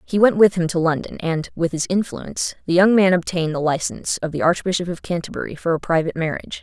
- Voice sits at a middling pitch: Yes, medium, 170 Hz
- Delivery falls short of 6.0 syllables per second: No, 6.5 syllables/s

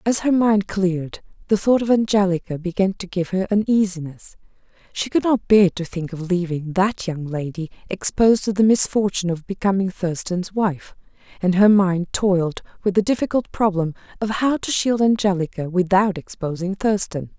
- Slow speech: No, average, 160 wpm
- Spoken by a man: No, female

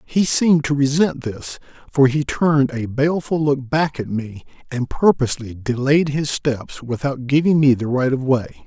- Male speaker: Yes, male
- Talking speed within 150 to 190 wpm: Yes, average, 180 wpm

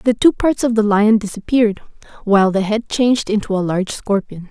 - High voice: Yes, high, 215 Hz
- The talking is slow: No, average, 200 wpm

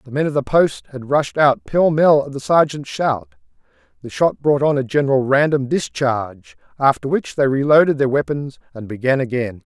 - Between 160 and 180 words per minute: No, average, 190 wpm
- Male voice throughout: Yes, male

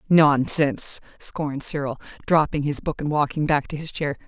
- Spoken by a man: No, female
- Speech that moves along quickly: No, average, 170 wpm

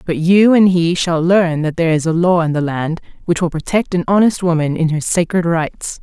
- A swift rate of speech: Yes, fast, 240 wpm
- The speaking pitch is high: No, medium, 170 Hz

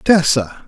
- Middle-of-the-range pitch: Yes, medium, 145 Hz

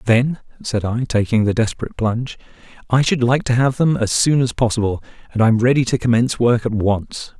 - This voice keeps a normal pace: No, fast, 210 wpm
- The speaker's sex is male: Yes, male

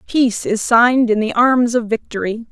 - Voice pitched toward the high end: Yes, high, 230 Hz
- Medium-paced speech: Yes, average, 190 wpm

